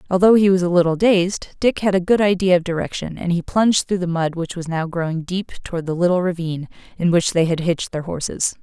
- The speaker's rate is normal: No, fast, 245 wpm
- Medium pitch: Yes, medium, 175 Hz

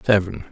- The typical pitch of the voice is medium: No, very low, 90 Hz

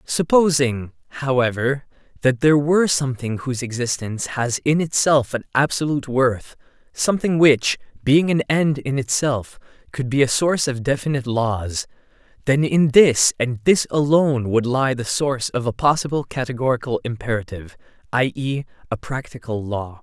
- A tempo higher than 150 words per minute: No, average, 145 wpm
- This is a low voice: Yes, low, 130 Hz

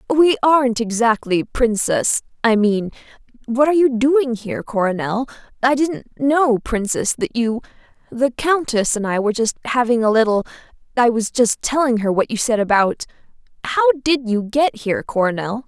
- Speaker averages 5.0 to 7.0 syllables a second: Yes, 5.1 syllables/s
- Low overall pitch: No, high, 240 Hz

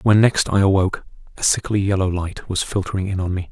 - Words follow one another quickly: Yes, fast, 220 wpm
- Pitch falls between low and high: No, very low, 95 Hz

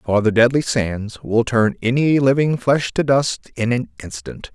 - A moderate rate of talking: Yes, average, 185 wpm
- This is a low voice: Yes, low, 120 Hz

